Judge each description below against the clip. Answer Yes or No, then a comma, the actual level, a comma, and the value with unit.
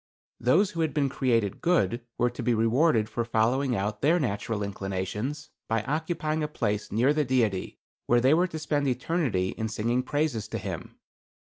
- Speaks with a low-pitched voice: Yes, low, 125 Hz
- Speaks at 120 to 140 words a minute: No, average, 175 wpm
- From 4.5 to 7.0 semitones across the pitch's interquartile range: Yes, wide, 5.5 semitones